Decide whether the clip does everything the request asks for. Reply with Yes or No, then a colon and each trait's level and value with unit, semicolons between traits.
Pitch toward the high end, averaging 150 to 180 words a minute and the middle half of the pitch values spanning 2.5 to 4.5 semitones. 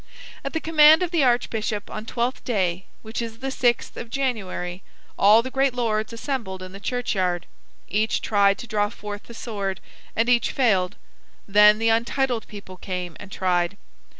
Yes: high, 220 Hz; average, 170 wpm; average, 3.8 semitones